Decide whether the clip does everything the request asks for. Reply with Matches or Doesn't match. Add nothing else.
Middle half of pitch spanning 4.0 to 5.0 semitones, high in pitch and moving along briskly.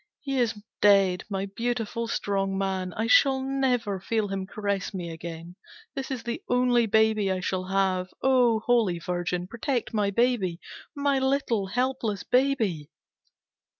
Doesn't match